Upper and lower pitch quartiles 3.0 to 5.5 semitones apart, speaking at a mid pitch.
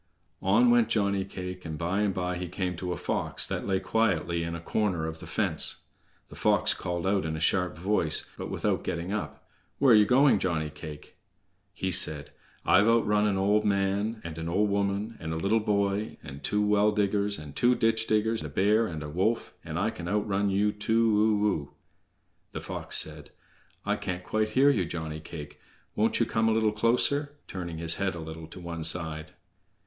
No: average, 4.2 semitones; very low, 95 Hz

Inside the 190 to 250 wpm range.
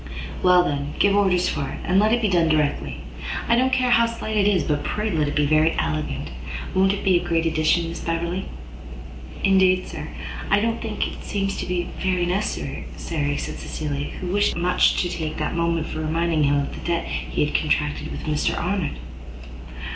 Yes: average, 200 wpm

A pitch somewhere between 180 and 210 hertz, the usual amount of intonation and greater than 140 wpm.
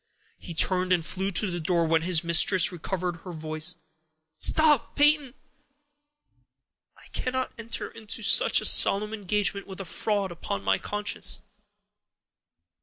No: high, 190 Hz; average, 3.8 semitones; slow, 135 wpm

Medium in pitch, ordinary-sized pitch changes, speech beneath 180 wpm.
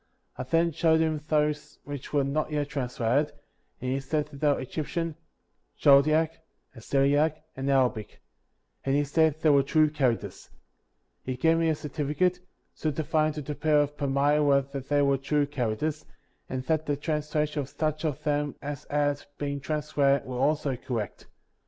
No: medium, 145 Hz; narrow, 1.9 semitones; average, 165 wpm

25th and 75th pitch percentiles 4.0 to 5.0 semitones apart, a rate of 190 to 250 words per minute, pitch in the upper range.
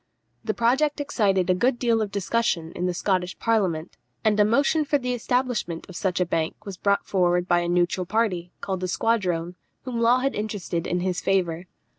Yes: average, 4.6 semitones; average, 195 wpm; high, 195 Hz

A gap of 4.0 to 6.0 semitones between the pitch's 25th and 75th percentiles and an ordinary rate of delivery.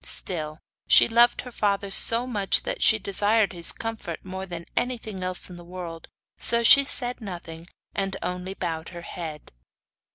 Yes: average, 4.6 semitones; average, 165 wpm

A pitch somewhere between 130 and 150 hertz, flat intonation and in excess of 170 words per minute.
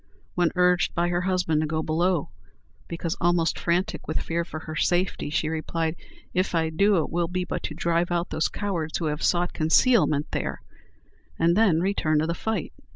No: medium, 170 Hz; narrow, 2.2 semitones; average, 190 wpm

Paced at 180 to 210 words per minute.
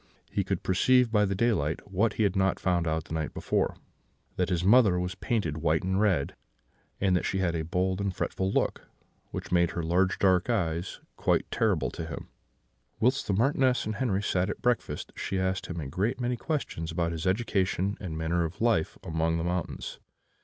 Yes: average, 195 wpm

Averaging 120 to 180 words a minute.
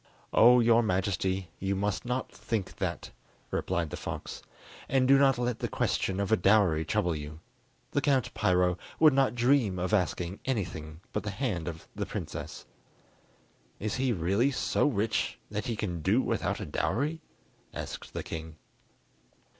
Yes: average, 160 wpm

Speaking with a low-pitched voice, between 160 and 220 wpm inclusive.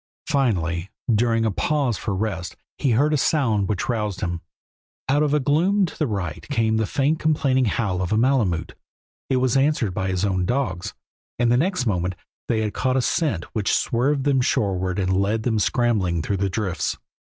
Yes: low, 110 Hz; average, 190 wpm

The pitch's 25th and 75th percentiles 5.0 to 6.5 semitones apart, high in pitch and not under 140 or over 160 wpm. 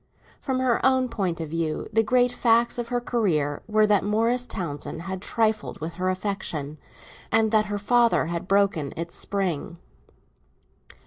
Yes: wide, 5.4 semitones; high, 205 Hz; average, 155 wpm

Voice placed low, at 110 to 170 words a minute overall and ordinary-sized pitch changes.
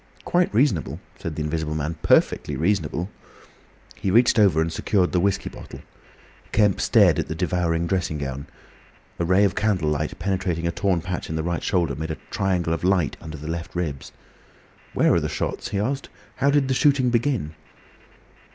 No: very low, 90 Hz; average, 180 wpm; average, 4.2 semitones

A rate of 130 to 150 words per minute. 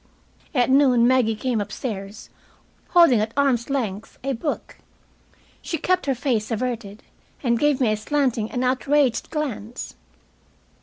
Yes: slow, 135 wpm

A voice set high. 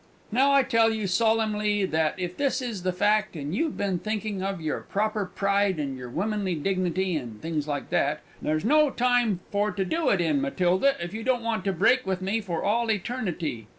Yes: high, 200 Hz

